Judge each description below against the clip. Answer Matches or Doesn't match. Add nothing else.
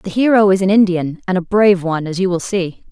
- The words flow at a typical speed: Doesn't match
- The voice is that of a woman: Matches